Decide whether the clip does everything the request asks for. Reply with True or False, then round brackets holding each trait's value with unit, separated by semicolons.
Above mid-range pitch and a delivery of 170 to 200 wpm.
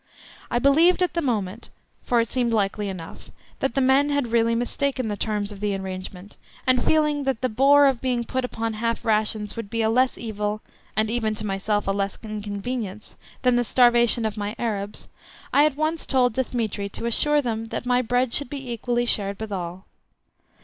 True (230 Hz; 195 wpm)